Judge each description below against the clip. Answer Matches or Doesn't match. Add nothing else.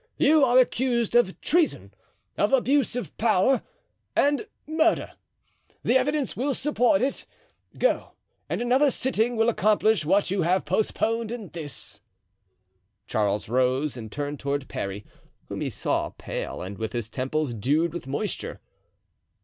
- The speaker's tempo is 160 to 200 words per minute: Doesn't match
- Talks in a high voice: Matches